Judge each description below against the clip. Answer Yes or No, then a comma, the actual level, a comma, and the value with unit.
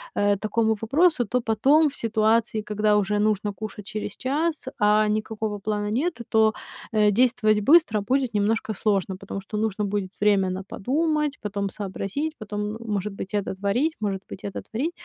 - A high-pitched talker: Yes, high, 215 Hz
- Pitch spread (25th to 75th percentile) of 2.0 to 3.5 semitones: Yes, narrow, 2.5 semitones